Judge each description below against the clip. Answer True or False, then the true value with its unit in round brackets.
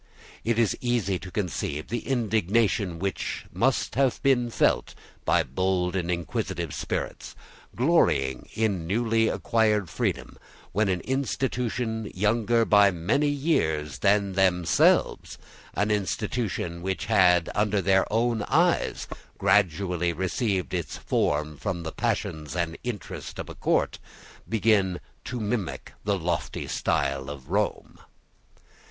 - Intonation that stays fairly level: False (4.4 semitones)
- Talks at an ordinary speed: False (120 wpm)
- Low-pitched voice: True (100 Hz)